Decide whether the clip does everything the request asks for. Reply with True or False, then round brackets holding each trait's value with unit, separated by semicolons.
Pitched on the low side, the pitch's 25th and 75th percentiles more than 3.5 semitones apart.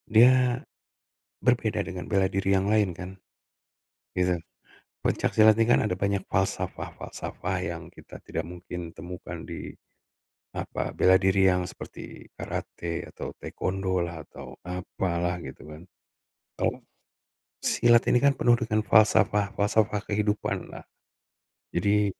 False (95 Hz; 3.2 semitones)